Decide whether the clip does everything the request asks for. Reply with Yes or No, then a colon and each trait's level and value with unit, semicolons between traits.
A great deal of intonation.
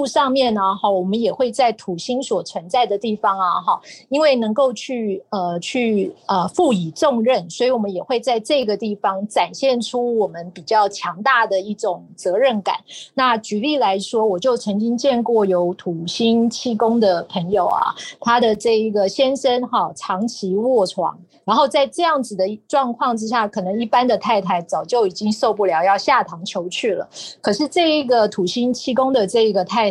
No: average, 4.5 semitones